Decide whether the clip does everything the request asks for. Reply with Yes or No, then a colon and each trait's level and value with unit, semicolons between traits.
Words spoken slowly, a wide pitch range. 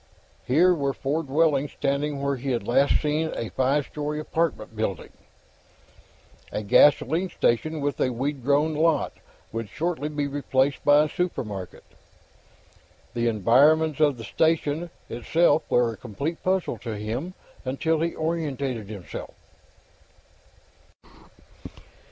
No: slow, 125 wpm; average, 4.3 semitones